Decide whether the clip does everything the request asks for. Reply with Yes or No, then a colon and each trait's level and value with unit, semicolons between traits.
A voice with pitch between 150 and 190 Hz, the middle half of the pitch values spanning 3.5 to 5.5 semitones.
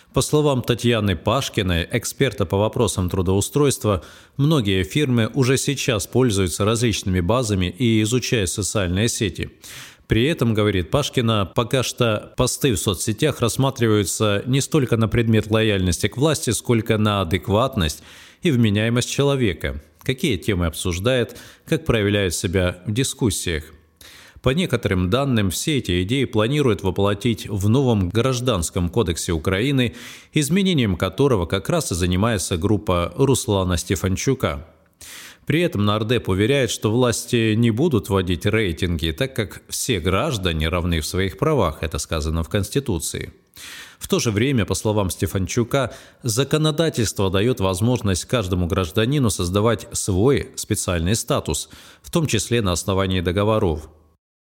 No: low, 110 Hz; average, 5.0 semitones